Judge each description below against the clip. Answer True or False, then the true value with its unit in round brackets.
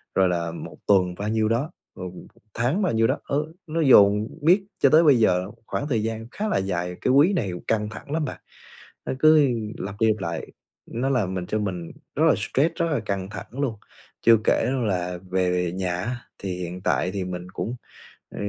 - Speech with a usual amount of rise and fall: False (7.0 semitones)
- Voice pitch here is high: False (105 Hz)